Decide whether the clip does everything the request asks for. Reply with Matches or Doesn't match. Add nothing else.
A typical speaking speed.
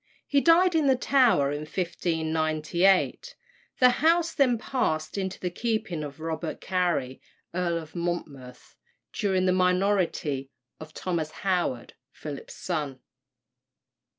Doesn't match